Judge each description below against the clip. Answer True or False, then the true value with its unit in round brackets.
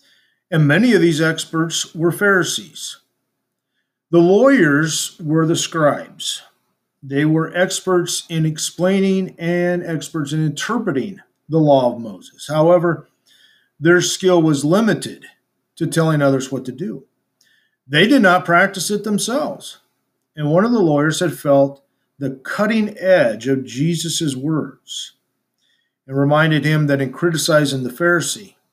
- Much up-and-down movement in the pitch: False (3.5 semitones)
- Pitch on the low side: False (160 Hz)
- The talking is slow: True (130 wpm)